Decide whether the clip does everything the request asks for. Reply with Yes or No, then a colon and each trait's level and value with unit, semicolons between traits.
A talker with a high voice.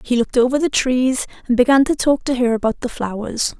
Yes: very high, 250 Hz